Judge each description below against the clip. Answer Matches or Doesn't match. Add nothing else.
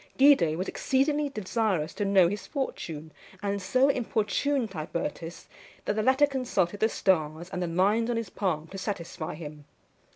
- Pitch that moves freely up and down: Matches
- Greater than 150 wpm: Matches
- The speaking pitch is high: Matches